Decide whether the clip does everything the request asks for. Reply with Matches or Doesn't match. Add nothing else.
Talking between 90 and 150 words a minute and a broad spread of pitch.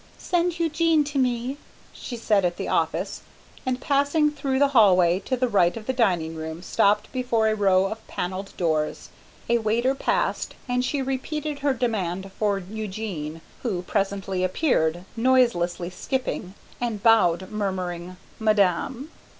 Matches